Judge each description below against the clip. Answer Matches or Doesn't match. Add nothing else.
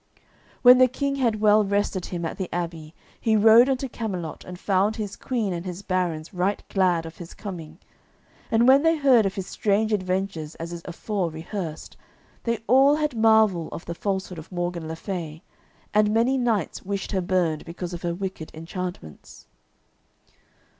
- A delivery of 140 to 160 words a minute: Doesn't match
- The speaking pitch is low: Doesn't match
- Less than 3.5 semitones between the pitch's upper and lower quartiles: Doesn't match